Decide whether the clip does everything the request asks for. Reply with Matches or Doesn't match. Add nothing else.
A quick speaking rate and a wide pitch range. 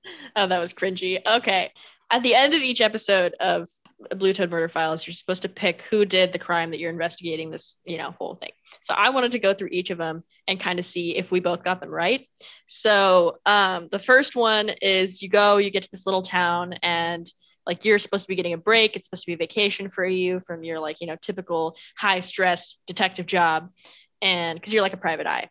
Doesn't match